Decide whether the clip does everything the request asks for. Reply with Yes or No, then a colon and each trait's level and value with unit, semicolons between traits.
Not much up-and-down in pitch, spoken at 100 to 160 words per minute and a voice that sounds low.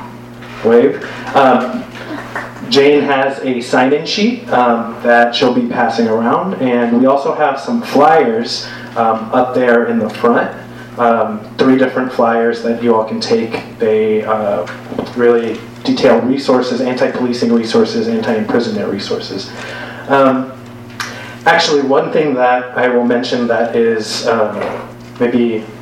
Yes: narrow, 1.9 semitones; slow, 135 wpm; low, 120 Hz